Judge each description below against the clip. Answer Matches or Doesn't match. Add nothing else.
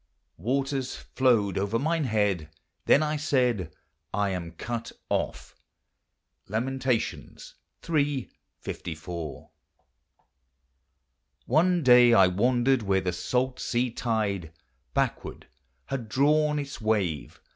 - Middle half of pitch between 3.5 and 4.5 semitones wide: Doesn't match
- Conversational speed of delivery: Doesn't match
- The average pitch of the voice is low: Matches